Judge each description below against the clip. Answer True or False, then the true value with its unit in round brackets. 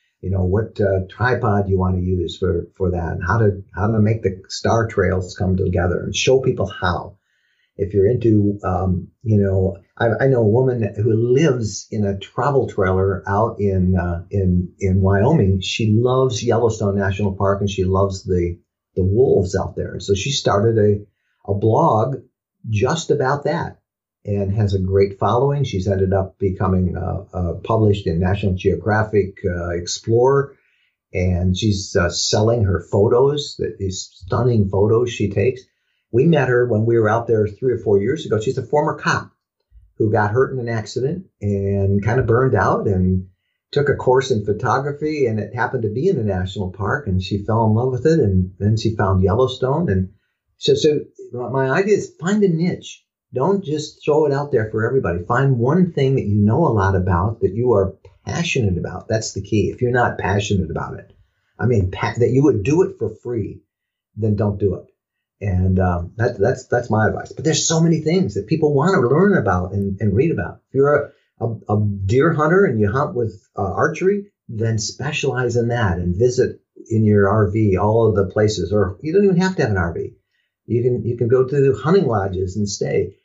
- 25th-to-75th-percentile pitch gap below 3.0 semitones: False (4.5 semitones)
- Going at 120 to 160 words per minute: False (200 wpm)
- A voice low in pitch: True (105 Hz)